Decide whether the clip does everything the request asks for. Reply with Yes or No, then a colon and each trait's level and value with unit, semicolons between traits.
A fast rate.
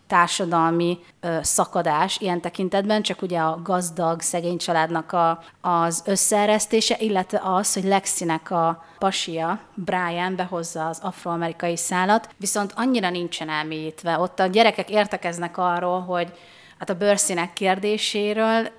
No: average, 125 wpm